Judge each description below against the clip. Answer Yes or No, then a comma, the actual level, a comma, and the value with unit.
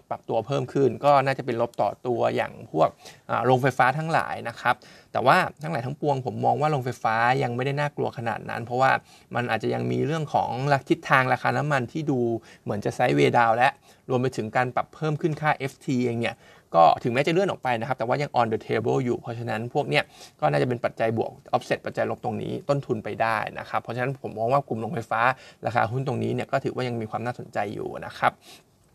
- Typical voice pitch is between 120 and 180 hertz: Yes, low, 125 Hz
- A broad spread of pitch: No, average, 3.2 semitones